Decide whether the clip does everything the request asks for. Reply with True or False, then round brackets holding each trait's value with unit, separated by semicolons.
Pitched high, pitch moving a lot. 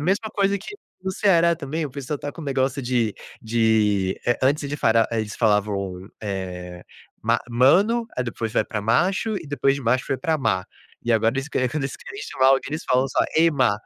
False (130 Hz; 5.7 semitones)